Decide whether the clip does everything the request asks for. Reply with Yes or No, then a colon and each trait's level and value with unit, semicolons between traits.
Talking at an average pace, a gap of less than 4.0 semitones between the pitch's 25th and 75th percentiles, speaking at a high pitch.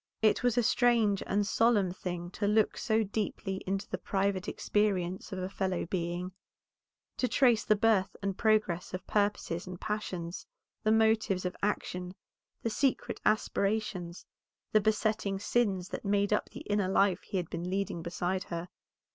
Yes: average, 160 wpm; average, 2.8 semitones; high, 200 Hz